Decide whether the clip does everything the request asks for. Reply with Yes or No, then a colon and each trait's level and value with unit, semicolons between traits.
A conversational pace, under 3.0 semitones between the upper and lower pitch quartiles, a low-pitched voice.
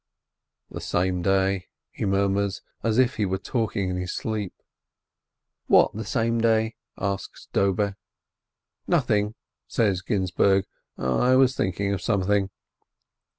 No: slow, 130 wpm; narrow, 2.6 semitones; low, 100 Hz